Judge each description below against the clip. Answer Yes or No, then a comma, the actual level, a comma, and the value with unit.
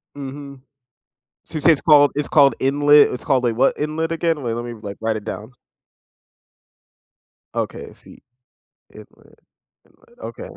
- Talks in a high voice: No, medium, 140 Hz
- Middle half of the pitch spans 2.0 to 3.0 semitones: No, average, 4.0 semitones